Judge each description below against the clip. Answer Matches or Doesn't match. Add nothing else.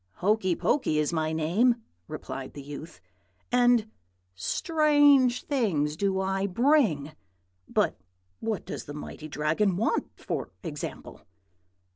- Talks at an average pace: Doesn't match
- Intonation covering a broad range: Matches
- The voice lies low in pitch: Doesn't match